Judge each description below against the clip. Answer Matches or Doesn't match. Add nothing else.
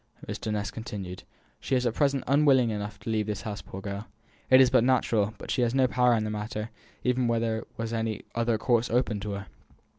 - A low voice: Matches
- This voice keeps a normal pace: Doesn't match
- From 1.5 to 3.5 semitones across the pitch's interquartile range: Matches